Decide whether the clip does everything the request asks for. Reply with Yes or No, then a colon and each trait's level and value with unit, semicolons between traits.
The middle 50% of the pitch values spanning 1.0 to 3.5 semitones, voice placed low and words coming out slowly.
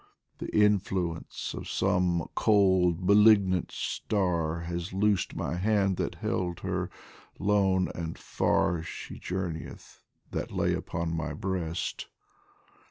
Yes: narrow, 2.6 semitones; very low, 90 Hz; slow, 110 wpm